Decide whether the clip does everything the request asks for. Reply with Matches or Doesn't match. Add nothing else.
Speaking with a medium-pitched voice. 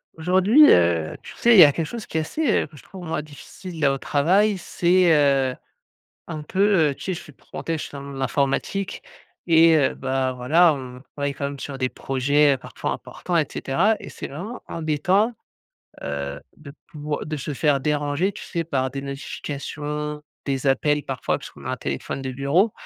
Matches